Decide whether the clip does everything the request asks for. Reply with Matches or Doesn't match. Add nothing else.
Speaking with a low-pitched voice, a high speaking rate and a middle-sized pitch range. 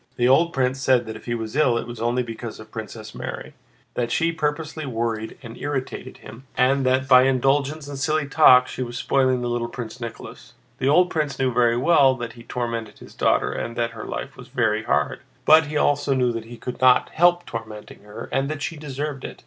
Matches